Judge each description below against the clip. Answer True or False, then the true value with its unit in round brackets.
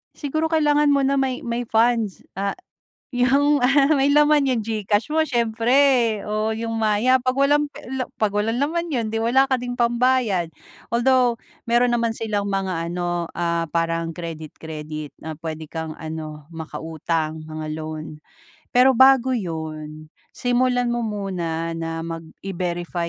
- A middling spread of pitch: False (7.5 semitones)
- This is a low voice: False (220 Hz)